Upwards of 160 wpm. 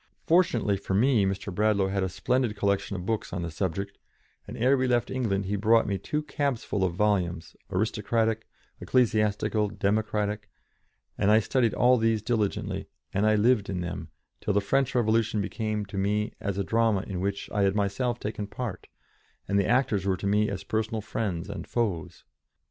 Yes: average, 180 wpm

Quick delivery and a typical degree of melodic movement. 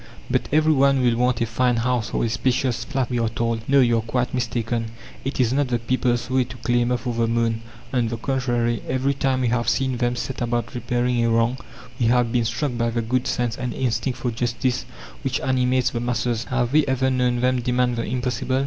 No: fast, 220 wpm; narrow, 1.6 semitones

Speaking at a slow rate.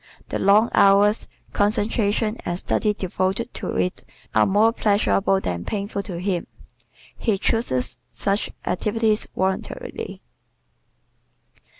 Yes: slow, 105 wpm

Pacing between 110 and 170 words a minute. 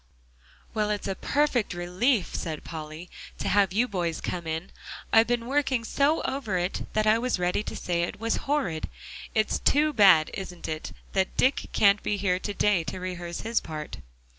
No: average, 185 wpm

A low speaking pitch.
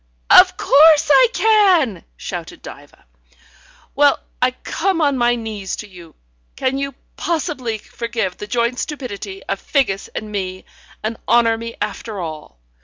No: high, 235 Hz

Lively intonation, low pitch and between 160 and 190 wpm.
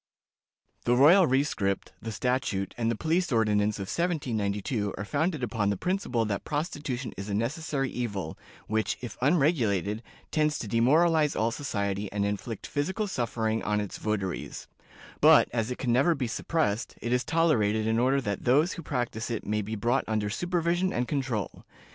Yes: wide, 5.7 semitones; low, 120 Hz; average, 165 wpm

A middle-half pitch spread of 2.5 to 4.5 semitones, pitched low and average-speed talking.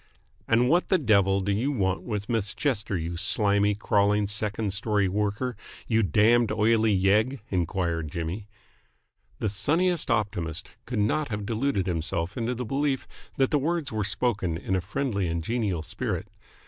Yes: average, 3.8 semitones; low, 105 Hz; average, 160 wpm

